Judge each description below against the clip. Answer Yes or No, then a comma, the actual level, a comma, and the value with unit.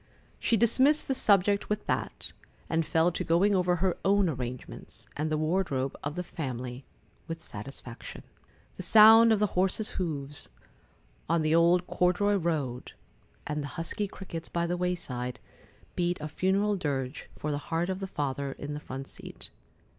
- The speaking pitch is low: No, medium, 170 Hz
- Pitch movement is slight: No, average, 4.9 semitones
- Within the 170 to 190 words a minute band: No, average, 160 wpm